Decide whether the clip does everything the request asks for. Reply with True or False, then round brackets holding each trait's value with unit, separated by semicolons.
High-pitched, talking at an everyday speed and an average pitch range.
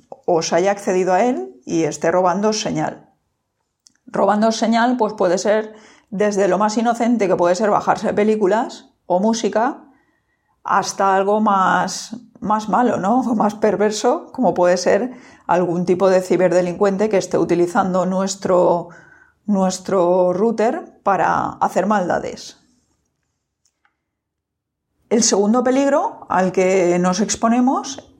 False (200 Hz; 120 wpm; 3.7 semitones)